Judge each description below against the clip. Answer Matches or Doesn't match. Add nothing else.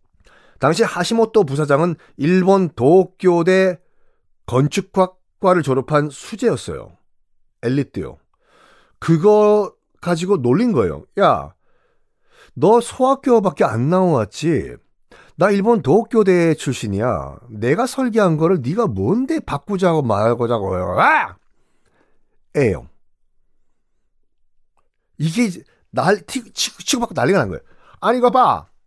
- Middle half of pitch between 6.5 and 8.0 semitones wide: Matches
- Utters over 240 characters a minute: Doesn't match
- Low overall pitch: Doesn't match